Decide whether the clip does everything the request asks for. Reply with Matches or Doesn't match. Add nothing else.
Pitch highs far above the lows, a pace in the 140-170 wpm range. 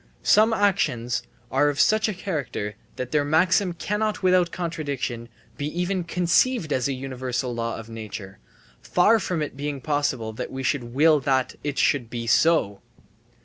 Matches